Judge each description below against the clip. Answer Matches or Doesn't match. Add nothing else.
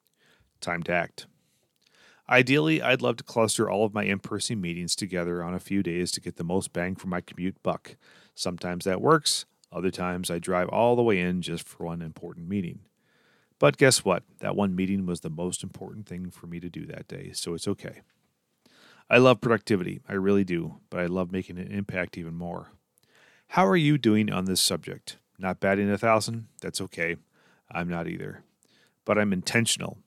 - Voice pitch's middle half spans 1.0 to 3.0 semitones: Doesn't match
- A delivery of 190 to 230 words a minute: Matches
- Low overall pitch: Matches